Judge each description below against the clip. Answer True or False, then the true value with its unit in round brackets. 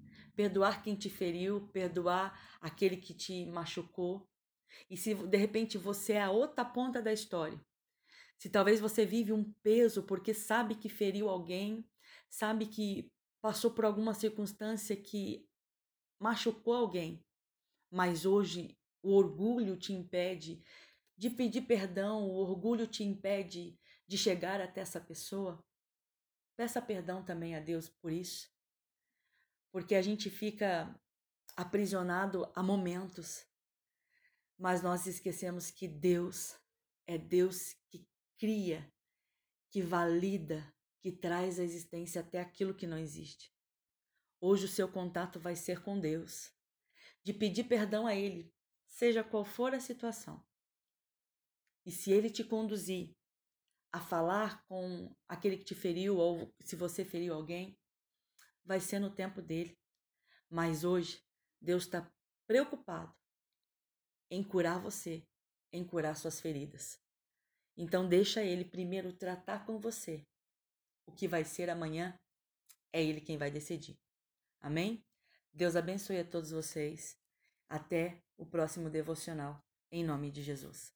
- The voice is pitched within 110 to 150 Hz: False (185 Hz)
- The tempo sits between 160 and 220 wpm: False (130 wpm)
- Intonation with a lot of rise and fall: False (3.4 semitones)